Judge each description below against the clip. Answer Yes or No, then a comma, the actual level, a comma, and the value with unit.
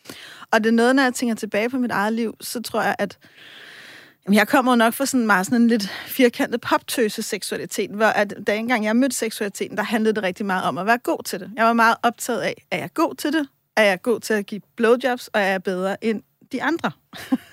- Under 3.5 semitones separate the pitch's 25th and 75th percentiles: Yes, average, 2.8 semitones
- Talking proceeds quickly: Yes, fast, 245 wpm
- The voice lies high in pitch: Yes, high, 225 Hz